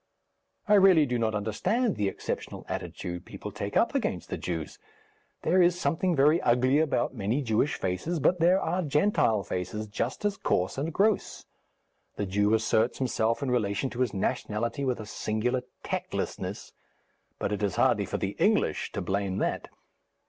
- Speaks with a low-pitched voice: Yes, low, 120 Hz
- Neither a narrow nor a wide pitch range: No, wide, 7.3 semitones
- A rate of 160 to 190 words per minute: Yes, average, 165 wpm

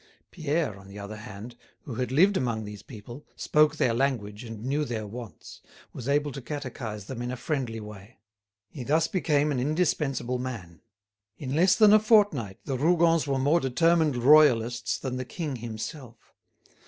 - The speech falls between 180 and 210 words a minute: No, average, 170 wpm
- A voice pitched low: Yes, low, 130 Hz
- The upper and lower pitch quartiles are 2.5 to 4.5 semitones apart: No, average, 5.0 semitones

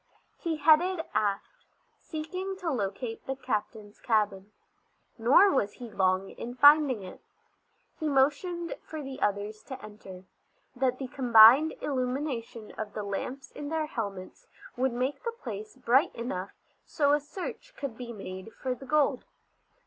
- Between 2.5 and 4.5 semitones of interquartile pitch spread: No, wide, 5.6 semitones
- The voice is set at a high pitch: Yes, very high, 255 Hz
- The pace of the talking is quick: No, average, 145 wpm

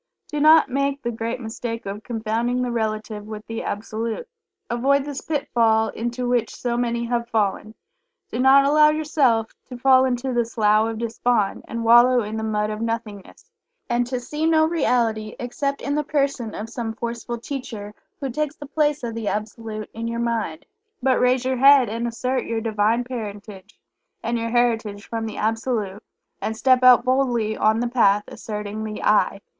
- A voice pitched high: Yes, high, 235 Hz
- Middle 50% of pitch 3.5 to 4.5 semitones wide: No, average, 2.7 semitones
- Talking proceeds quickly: No, average, 180 wpm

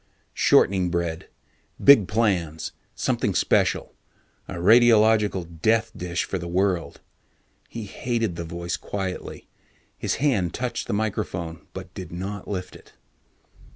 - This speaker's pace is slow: Yes, slow, 120 wpm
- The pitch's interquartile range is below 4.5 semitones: Yes, average, 4.1 semitones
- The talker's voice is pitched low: Yes, very low, 95 Hz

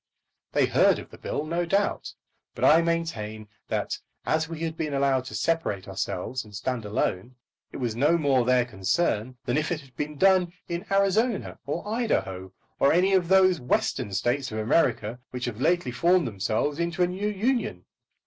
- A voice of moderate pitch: Yes, medium, 145 Hz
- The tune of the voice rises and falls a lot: Yes, wide, 6.7 semitones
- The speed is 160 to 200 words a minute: Yes, average, 180 wpm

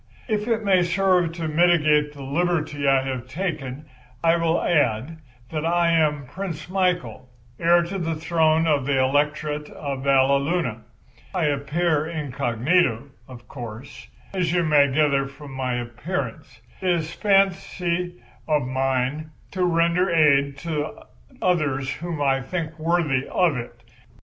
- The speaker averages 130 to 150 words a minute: Yes, average, 140 wpm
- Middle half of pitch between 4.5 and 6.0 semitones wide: No, average, 4.0 semitones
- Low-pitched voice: No, medium, 155 Hz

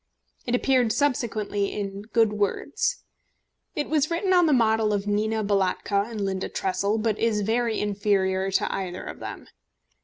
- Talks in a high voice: Yes, high, 215 Hz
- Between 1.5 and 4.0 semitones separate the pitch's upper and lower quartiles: Yes, average, 2.9 semitones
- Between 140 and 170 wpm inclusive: Yes, average, 155 wpm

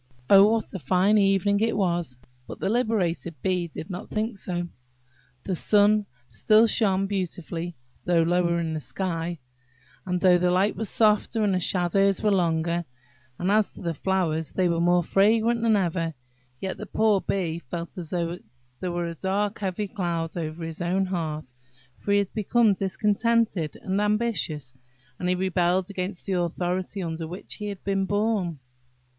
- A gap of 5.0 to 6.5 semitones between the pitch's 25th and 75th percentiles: No, average, 2.9 semitones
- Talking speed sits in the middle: Yes, average, 170 wpm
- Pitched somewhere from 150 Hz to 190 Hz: Yes, medium, 185 Hz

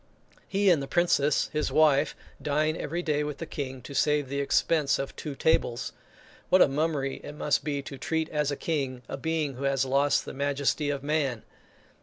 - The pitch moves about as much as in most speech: No, narrow, 2.2 semitones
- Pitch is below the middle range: No, medium, 145 Hz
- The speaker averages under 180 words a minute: No, average, 195 wpm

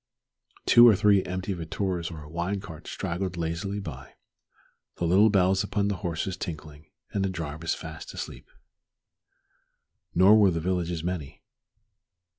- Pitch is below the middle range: Yes, very low, 90 Hz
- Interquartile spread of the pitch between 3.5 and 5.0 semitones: No, average, 2.9 semitones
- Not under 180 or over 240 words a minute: No, average, 140 wpm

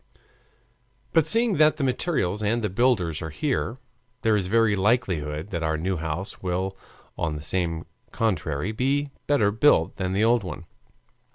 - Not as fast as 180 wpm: Yes, average, 155 wpm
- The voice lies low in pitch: Yes, low, 100 Hz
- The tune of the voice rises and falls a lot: Yes, wide, 6.1 semitones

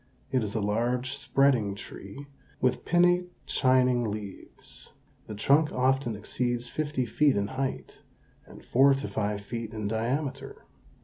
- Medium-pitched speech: No, low, 125 Hz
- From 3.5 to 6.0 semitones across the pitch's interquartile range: Yes, average, 4.1 semitones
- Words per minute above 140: No, slow, 135 wpm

